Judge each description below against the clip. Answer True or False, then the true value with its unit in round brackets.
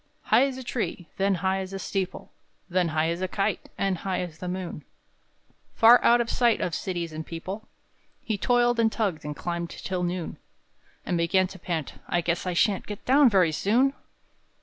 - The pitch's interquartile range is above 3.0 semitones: True (4.1 semitones)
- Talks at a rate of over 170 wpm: True (195 wpm)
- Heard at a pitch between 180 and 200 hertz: True (185 Hz)